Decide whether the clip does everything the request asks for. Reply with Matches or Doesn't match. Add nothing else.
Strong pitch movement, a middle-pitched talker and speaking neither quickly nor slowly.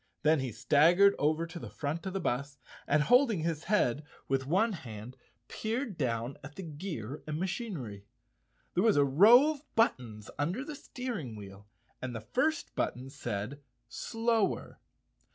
Matches